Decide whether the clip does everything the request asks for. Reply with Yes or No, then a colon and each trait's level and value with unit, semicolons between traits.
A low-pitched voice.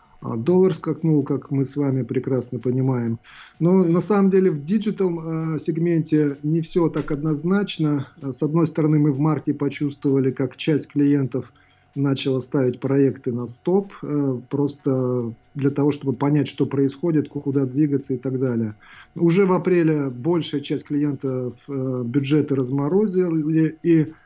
No: medium, 145 Hz